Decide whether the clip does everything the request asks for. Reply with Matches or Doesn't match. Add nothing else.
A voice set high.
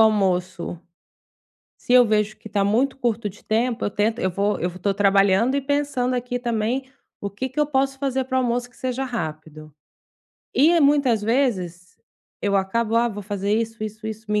Matches